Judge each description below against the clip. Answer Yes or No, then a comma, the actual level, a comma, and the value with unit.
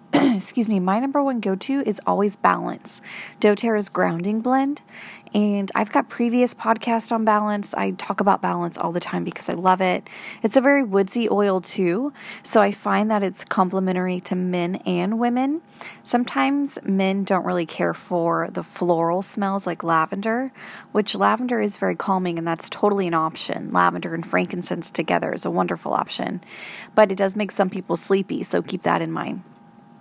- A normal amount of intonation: Yes, average, 3.7 semitones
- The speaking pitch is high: Yes, high, 200 Hz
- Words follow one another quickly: No, average, 175 wpm